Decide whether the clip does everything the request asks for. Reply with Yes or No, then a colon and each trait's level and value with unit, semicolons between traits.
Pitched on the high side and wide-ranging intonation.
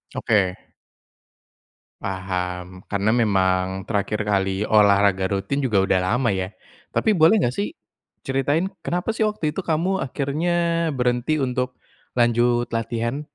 No: low, 120 Hz; wide, 6.9 semitones